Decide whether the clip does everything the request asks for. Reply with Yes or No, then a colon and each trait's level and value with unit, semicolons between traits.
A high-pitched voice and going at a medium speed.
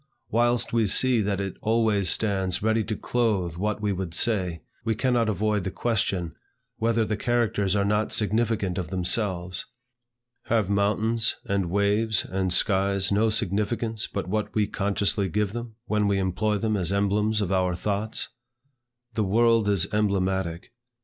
No: low, 105 Hz; average, 155 wpm